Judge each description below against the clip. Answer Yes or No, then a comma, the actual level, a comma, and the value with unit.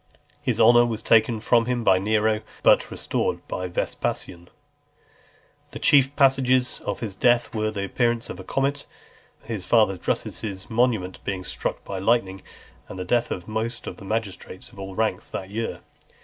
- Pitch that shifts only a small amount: No, average, 3.8 semitones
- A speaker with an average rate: Yes, average, 170 wpm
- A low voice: Yes, low, 110 Hz